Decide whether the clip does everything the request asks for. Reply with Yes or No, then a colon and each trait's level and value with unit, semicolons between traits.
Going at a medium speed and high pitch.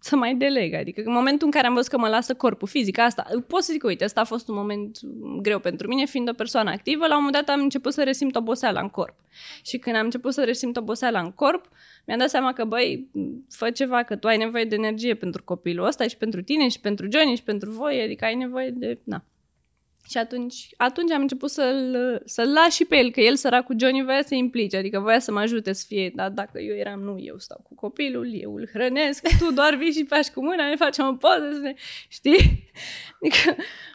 No: fast, 235 wpm; high, 245 Hz